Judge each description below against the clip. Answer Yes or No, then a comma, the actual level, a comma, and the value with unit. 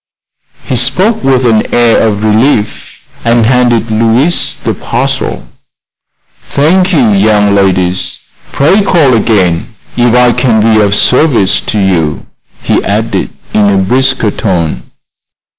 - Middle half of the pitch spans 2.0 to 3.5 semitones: No, average, 4.1 semitones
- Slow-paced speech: Yes, slow, 125 wpm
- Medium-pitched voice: No, low, 115 Hz